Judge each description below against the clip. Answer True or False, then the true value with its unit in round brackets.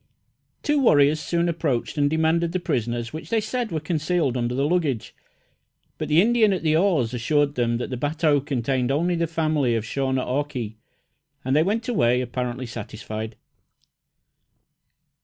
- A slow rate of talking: False (165 wpm)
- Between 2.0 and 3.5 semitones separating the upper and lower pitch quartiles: False (5.2 semitones)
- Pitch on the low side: False (145 Hz)